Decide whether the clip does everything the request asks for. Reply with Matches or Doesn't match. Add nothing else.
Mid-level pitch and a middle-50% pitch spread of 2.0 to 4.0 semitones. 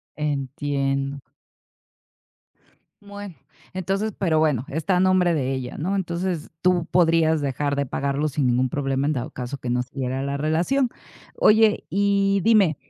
Doesn't match